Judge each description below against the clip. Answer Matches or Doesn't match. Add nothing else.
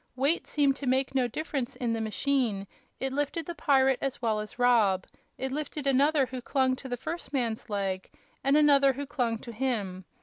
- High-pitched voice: Matches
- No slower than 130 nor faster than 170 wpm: Doesn't match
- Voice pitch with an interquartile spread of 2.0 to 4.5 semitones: Matches